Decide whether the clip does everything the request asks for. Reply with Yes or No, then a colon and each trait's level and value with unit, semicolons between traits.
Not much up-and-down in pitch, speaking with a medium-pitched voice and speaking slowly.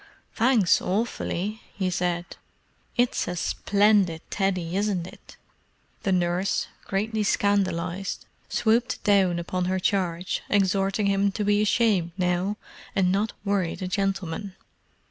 No: narrow, 2.3 semitones; high, 195 Hz; slow, 120 wpm